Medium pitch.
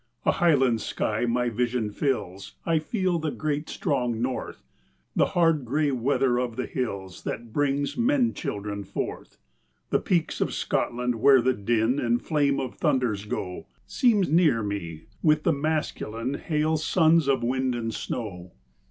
No: low, 130 Hz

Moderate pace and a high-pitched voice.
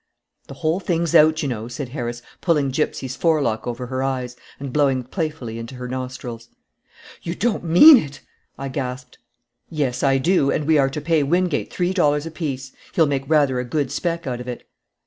No: average, 185 wpm; medium, 140 Hz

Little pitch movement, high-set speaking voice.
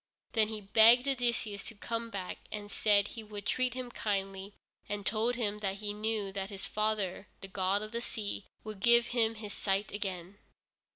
Yes: narrow, 2.2 semitones; high, 210 Hz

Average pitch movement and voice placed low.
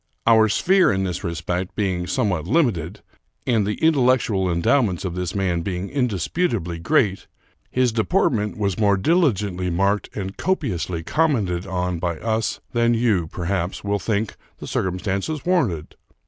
Yes: average, 4.7 semitones; low, 100 Hz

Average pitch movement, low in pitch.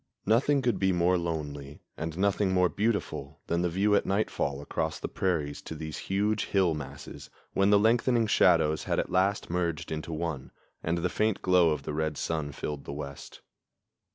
Yes: average, 4.3 semitones; very low, 85 Hz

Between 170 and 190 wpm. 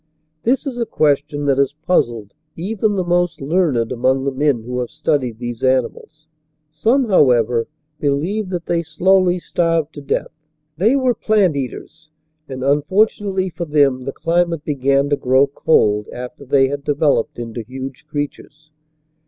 No: average, 160 wpm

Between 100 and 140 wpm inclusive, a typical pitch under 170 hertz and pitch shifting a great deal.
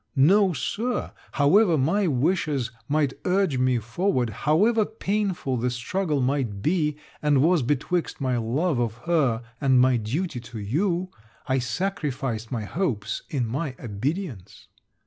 Yes: slow, 135 wpm; medium, 140 Hz; wide, 6.6 semitones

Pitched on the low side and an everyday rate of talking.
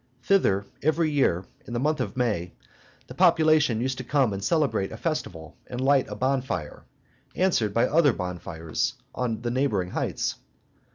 Yes: low, 125 Hz; average, 160 wpm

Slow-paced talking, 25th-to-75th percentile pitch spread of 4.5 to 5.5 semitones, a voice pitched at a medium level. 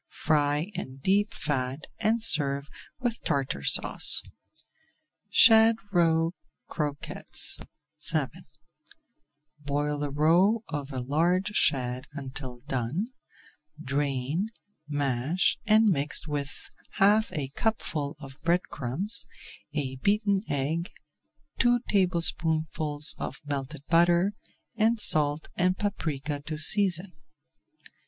Yes: slow, 100 wpm; average, 5.1 semitones; medium, 155 Hz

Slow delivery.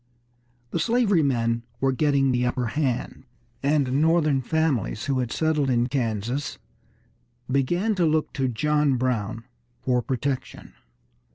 Yes: slow, 125 wpm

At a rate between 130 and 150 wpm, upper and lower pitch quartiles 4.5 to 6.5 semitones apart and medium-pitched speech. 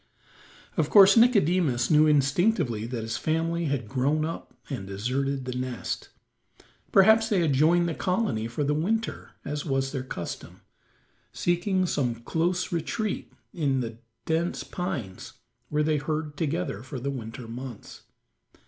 Yes: average, 140 wpm; average, 5.3 semitones; medium, 150 Hz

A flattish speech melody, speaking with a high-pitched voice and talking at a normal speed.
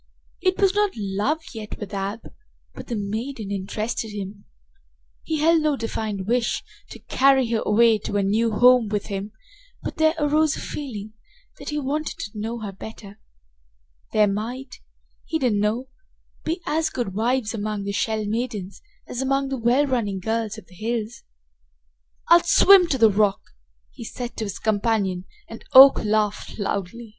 No: average, 4.2 semitones; high, 225 Hz; average, 165 wpm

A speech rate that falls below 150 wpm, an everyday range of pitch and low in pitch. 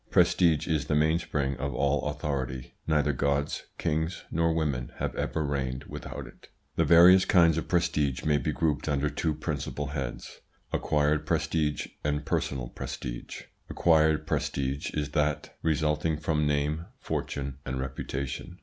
No: average, 140 wpm; narrow, 2.2 semitones; very low, 75 Hz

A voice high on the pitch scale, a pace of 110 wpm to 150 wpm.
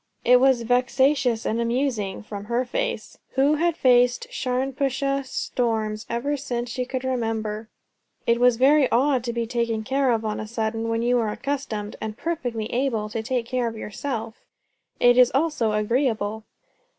No: high, 245 Hz; average, 165 wpm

